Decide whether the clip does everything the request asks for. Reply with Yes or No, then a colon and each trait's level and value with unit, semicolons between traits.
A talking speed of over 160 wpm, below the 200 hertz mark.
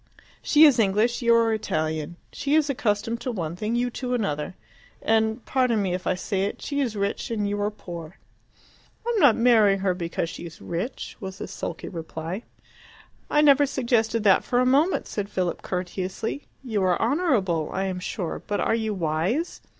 No: average, 190 wpm; high, 210 Hz